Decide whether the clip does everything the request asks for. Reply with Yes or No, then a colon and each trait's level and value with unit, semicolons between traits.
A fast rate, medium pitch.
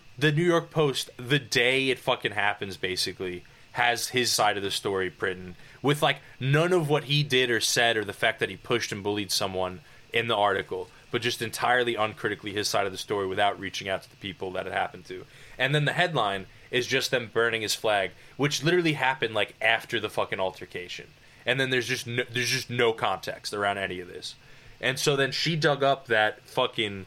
No: fast, 215 wpm; low, 120 Hz